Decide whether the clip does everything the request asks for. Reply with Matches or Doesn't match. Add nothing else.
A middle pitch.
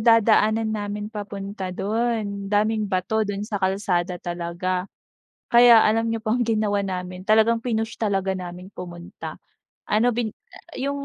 Doesn't match